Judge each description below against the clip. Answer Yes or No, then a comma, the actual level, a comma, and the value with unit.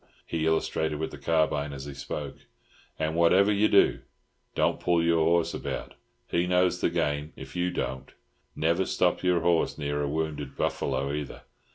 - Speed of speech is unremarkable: Yes, average, 170 wpm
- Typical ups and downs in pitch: Yes, average, 3.0 semitones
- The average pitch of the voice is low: Yes, very low, 80 Hz